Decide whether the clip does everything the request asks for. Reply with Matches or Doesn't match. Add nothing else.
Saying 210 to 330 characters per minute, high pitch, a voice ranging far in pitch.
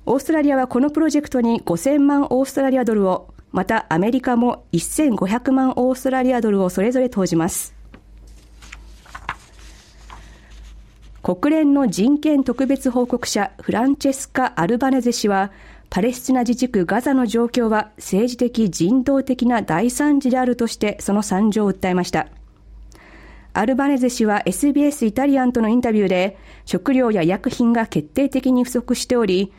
Doesn't match